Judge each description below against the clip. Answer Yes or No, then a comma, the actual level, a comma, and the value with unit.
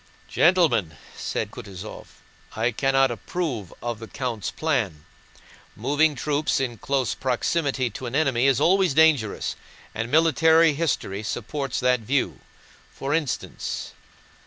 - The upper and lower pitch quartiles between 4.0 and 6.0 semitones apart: Yes, average, 4.9 semitones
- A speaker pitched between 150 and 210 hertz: No, low, 135 Hz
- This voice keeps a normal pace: No, slow, 120 wpm